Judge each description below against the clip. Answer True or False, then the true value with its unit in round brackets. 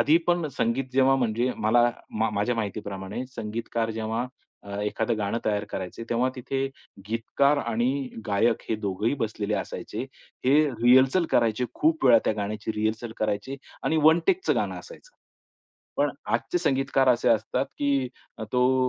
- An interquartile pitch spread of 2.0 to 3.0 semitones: False (3.6 semitones)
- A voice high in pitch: False (120 Hz)